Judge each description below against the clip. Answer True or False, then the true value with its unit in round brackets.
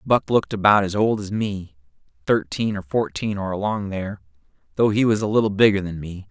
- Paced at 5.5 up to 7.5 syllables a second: True (5.6 syllables/s)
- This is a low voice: True (100 Hz)